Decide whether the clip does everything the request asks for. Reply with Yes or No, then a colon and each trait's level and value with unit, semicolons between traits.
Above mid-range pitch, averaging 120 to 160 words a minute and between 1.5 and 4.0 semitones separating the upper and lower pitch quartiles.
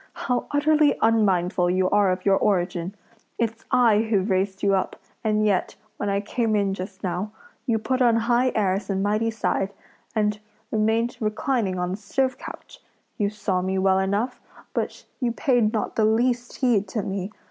No: high, 210 Hz; average, 170 wpm; average, 3.1 semitones